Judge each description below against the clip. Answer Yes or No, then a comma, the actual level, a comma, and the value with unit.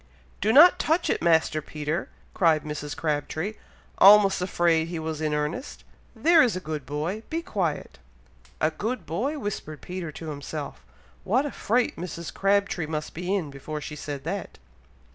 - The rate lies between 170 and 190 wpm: No, average, 160 wpm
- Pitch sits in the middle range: Yes, medium, 165 Hz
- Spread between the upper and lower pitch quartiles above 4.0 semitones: Yes, average, 4.8 semitones